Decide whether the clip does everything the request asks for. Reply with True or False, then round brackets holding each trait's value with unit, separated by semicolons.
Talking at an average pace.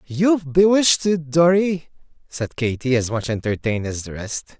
True (155 wpm)